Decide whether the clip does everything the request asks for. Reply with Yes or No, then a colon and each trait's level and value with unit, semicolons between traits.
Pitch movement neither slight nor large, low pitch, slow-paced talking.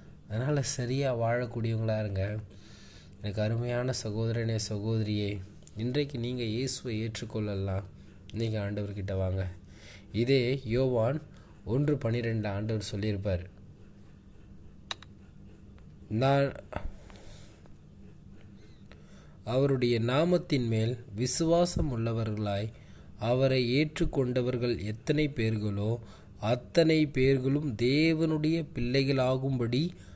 Yes: average, 4.2 semitones; low, 115 Hz; slow, 70 wpm